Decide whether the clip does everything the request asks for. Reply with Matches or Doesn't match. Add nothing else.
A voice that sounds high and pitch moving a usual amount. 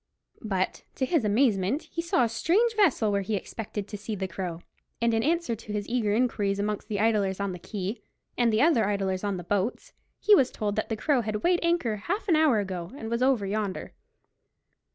Matches